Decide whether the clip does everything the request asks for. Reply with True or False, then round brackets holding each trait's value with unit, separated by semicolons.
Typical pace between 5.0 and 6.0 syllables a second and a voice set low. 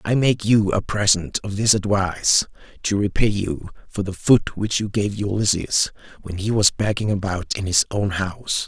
False (4.7 syllables/s; 100 Hz)